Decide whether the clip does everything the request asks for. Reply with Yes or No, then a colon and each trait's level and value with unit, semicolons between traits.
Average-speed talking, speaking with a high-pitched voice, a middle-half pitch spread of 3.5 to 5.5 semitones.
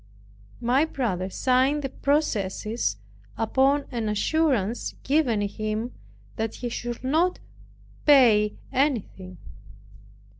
No: slow, 90 wpm; high, 240 Hz; average, 4.6 semitones